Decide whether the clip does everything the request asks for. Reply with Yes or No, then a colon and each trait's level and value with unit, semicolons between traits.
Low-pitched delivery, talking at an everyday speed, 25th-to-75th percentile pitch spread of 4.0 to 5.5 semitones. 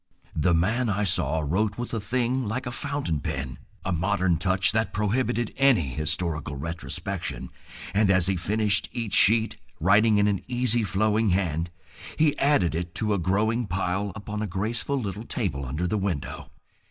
Yes: low, 100 Hz; average, 165 wpm; average, 4.6 semitones